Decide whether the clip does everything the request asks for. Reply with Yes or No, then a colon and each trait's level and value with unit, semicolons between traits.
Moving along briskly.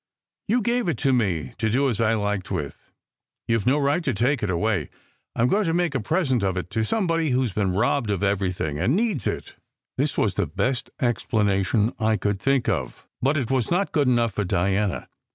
Yes: fast, 220 wpm